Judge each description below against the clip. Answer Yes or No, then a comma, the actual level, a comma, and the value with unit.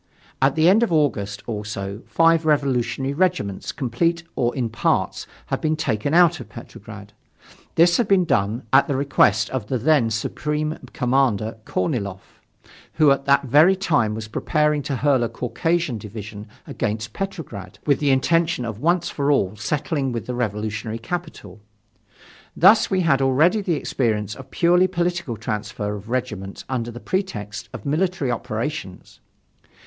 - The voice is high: No, low, 135 Hz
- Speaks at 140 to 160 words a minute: Yes, average, 155 wpm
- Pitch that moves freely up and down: Yes, wide, 6.7 semitones